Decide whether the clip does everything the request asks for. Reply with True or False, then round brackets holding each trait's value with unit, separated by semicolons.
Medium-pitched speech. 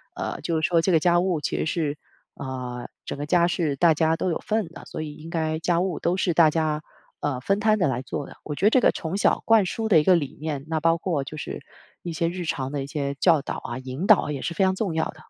True (160 Hz)